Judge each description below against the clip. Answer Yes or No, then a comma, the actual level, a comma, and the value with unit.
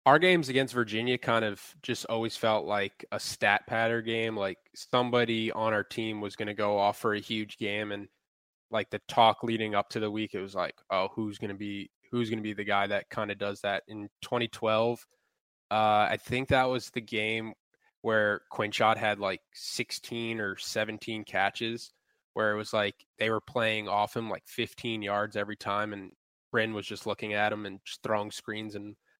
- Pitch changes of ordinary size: No, narrow, 1.7 semitones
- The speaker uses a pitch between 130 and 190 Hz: No, low, 110 Hz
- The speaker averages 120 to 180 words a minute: No, fast, 205 wpm